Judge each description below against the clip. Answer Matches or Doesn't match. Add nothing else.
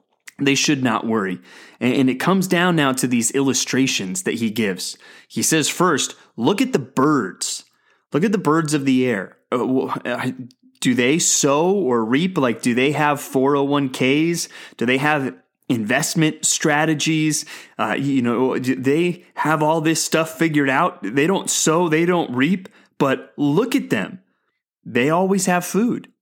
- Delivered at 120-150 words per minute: Doesn't match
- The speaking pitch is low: Doesn't match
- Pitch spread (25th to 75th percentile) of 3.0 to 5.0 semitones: Matches